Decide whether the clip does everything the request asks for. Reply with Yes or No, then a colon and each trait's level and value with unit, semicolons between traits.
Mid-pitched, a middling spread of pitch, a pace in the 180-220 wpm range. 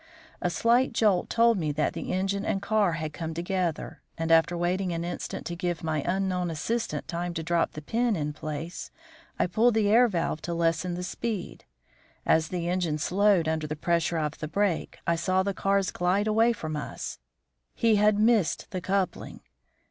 Yes: medium, 180 Hz; average, 3.6 semitones; average, 185 wpm